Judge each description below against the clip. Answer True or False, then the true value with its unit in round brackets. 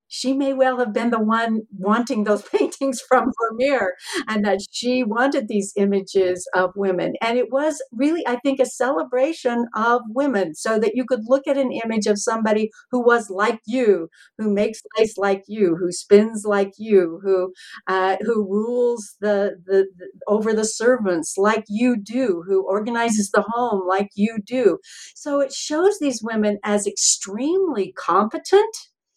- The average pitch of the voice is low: False (220 Hz)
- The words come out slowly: False (165 wpm)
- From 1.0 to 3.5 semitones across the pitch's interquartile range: False (4.0 semitones)